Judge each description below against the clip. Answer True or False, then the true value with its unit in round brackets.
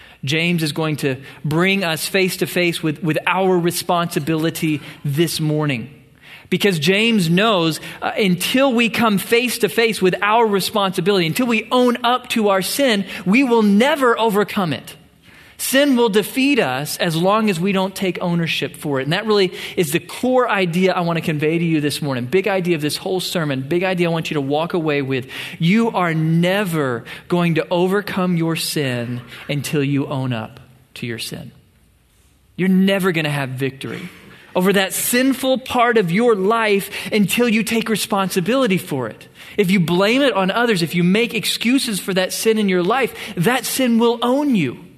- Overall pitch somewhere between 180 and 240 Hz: True (185 Hz)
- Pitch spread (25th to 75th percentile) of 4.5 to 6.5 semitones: True (5.2 semitones)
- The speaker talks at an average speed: True (185 wpm)